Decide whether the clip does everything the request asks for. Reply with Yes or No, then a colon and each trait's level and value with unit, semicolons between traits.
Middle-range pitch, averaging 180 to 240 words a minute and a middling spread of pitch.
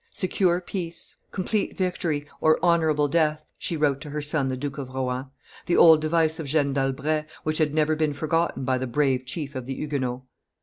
Yes: medium, 150 Hz; average, 190 wpm; average, 3.1 semitones